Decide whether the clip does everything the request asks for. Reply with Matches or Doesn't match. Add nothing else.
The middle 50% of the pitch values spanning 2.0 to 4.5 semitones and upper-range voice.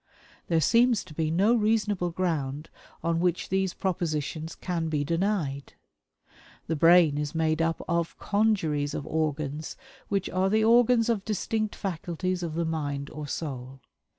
Doesn't match